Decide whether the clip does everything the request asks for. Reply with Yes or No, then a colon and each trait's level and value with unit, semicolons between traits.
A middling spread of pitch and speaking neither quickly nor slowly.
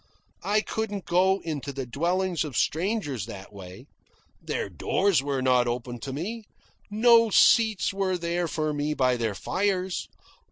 No: wide, 7.0 semitones; average, 150 wpm